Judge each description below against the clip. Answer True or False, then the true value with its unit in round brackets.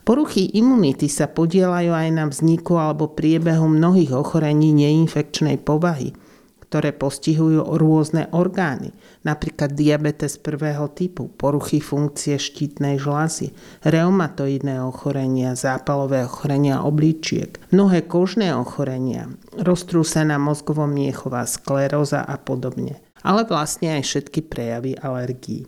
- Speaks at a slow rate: True (105 wpm)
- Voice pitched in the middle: True (150 Hz)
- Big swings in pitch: False (2.7 semitones)